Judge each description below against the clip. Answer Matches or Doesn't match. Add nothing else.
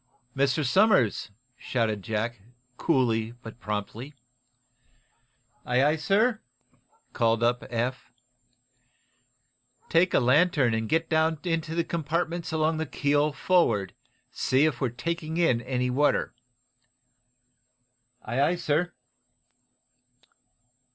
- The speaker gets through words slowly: Matches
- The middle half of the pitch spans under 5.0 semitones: Doesn't match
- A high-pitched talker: Doesn't match